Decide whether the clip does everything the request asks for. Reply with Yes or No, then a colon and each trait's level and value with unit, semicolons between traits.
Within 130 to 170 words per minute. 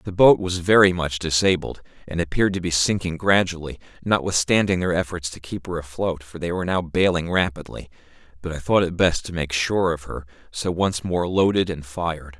No: average, 195 wpm